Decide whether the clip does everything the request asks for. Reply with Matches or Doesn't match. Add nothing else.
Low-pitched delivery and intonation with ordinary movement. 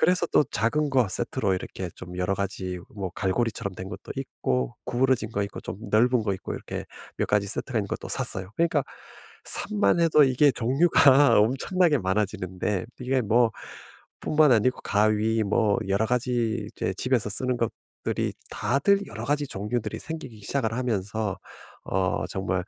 Matches